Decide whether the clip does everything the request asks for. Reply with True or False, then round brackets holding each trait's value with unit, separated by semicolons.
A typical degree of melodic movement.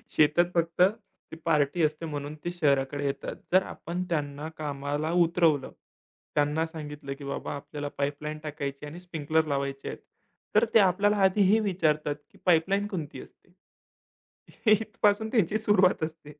True (3.7 semitones)